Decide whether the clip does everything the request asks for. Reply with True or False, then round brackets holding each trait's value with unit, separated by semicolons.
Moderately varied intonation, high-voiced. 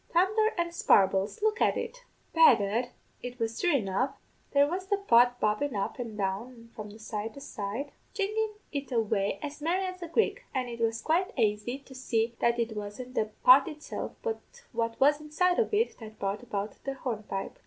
False (7.4 semitones; 250 Hz)